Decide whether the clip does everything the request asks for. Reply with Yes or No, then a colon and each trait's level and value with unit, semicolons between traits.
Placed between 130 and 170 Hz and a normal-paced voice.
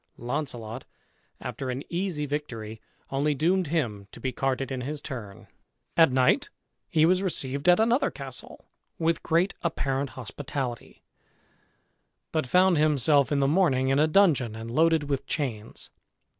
Yes: medium, 140 Hz; average, 145 wpm